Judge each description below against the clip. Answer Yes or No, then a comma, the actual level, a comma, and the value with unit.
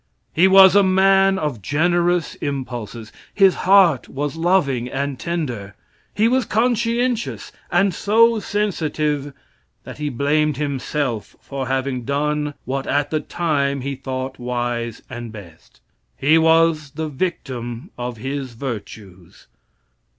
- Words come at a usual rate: No, slow, 125 wpm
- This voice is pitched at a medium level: Yes, medium, 145 Hz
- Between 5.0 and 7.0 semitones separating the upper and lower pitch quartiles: Yes, wide, 5.5 semitones